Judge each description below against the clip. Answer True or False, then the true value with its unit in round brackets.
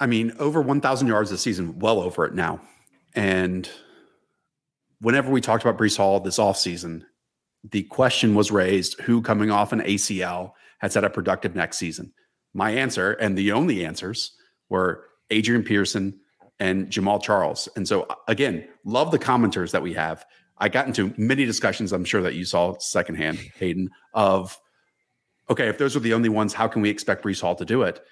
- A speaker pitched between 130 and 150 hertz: False (105 Hz)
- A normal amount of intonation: True (3.1 semitones)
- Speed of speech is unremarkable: True (180 wpm)